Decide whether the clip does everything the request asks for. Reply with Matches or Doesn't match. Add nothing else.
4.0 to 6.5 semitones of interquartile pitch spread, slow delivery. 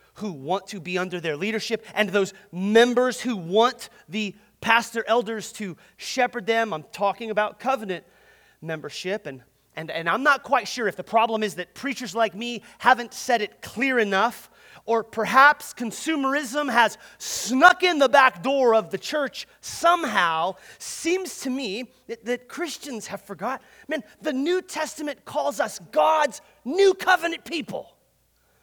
Doesn't match